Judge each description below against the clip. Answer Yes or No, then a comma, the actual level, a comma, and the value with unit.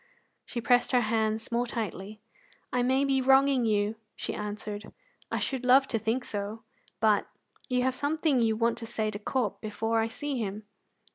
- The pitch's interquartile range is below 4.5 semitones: Yes, average, 2.9 semitones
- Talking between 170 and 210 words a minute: Yes, average, 180 wpm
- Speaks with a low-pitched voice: No, high, 230 Hz